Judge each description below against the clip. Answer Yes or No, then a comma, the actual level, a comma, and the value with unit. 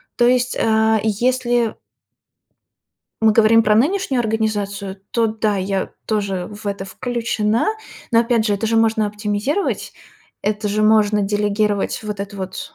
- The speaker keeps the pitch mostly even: Yes, narrow, 1.8 semitones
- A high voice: Yes, high, 215 Hz